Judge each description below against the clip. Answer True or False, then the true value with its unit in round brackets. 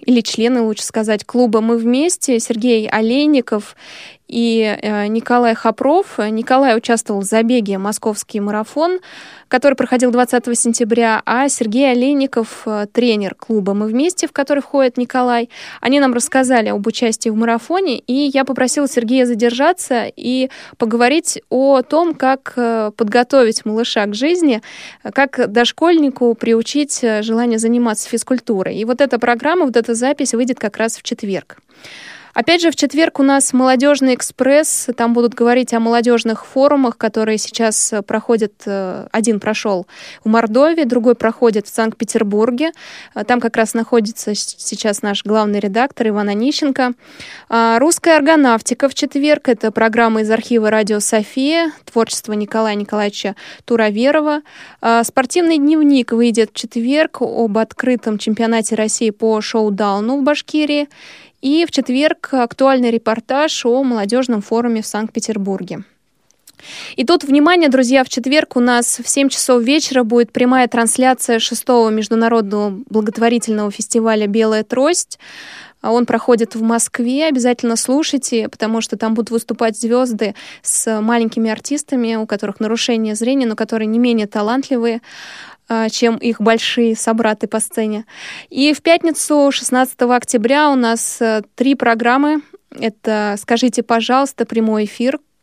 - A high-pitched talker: True (235 Hz)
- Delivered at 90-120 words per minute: False (135 wpm)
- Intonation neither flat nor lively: True (3.1 semitones)